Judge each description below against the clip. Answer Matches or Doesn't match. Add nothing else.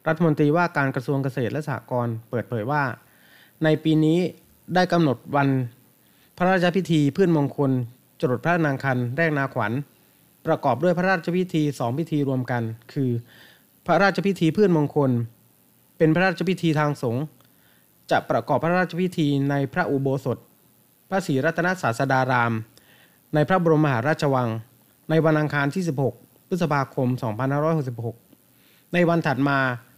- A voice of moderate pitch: Matches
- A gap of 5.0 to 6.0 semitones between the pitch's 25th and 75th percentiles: Doesn't match